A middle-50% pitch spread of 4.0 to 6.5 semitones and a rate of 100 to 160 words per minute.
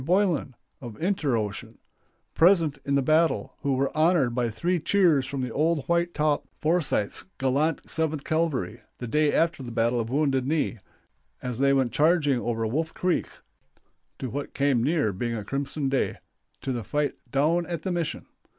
No: average, 4.3 semitones; average, 170 wpm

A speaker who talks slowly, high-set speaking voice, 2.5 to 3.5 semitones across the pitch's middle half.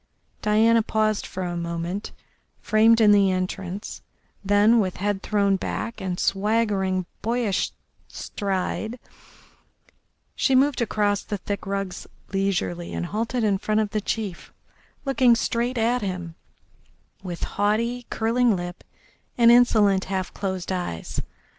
Yes: slow, 125 wpm; high, 205 Hz; average, 3.2 semitones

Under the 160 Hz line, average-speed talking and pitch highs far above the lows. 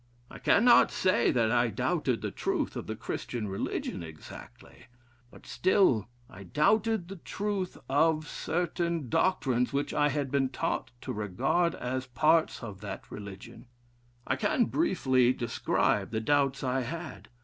Yes: medium, 140 Hz; average, 145 wpm; wide, 6.4 semitones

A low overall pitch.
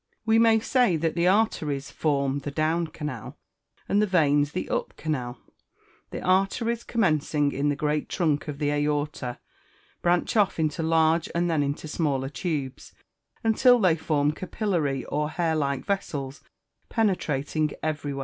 No: medium, 155 Hz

